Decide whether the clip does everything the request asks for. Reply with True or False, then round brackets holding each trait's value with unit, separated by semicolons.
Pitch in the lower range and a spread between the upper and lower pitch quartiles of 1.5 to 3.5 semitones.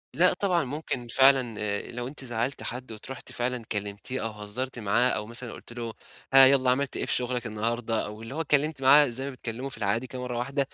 True (125 Hz; 2.8 semitones)